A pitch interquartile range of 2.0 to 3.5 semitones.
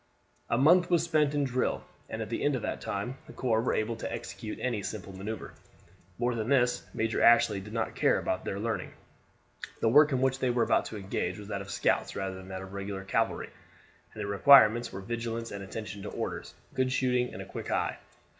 No: average, 4.2 semitones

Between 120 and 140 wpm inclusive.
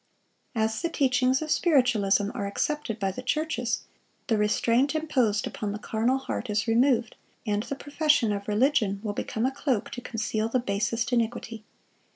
No: average, 165 wpm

